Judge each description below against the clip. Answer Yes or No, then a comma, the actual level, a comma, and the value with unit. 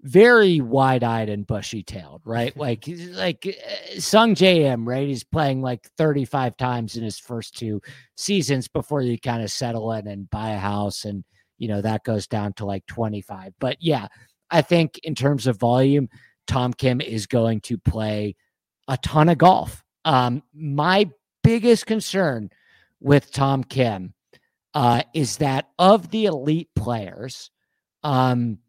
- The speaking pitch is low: Yes, low, 130 Hz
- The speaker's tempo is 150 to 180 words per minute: Yes, average, 155 wpm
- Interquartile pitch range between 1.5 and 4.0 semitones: No, wide, 5.6 semitones